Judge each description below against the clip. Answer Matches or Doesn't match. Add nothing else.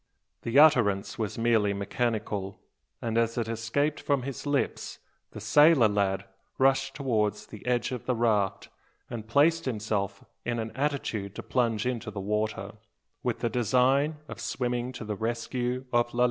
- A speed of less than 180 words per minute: Matches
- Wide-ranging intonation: Doesn't match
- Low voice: Matches